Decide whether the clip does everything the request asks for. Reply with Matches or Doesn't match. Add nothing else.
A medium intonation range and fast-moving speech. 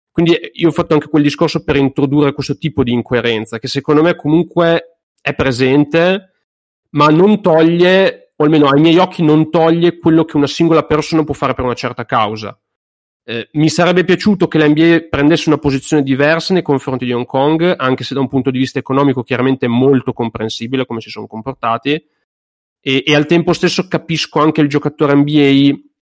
Matches